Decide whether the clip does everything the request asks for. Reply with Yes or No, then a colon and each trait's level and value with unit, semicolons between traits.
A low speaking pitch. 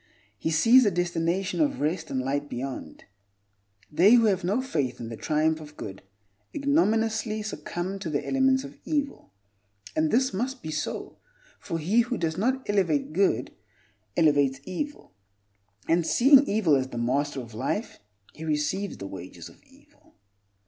No: medium, 175 Hz